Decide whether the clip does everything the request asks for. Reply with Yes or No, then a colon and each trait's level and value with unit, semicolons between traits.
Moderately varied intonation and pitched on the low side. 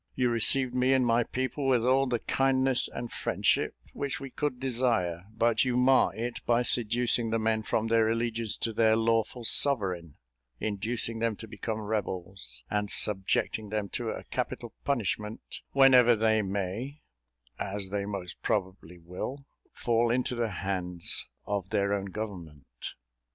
Yes: average, 3.5 semitones; low, 115 Hz